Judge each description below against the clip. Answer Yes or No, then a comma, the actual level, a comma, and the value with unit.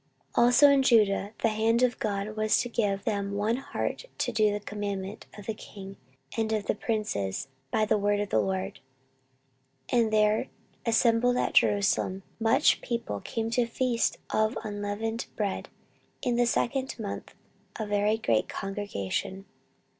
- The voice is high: Yes, high, 215 Hz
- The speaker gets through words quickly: No, average, 160 wpm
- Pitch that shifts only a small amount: Yes, narrow, 2.3 semitones